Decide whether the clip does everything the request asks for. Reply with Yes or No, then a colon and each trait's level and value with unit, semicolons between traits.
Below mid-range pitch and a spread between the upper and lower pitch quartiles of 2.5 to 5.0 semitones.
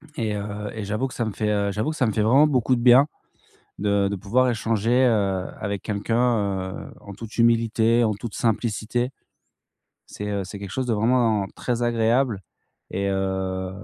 Yes: low, 110 Hz; average, 2.9 semitones